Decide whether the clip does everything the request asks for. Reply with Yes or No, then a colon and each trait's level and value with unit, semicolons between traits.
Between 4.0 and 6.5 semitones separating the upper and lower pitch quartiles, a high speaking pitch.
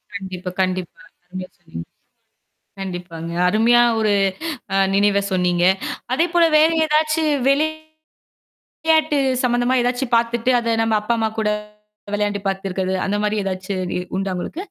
Yes: average, 4.6 semitones; high, 210 Hz